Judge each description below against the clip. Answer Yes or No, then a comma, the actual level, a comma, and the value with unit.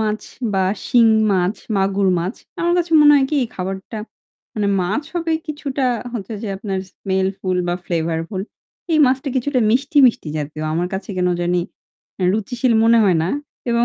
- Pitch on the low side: No, high, 205 Hz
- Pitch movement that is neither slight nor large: No, wide, 5.8 semitones